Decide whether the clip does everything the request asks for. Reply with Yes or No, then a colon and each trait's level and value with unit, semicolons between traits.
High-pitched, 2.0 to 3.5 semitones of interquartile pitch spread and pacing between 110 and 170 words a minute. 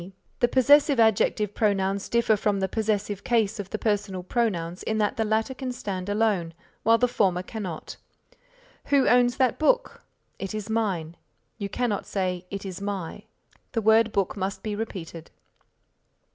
Yes: high, 210 Hz; average, 2.9 semitones; average, 160 wpm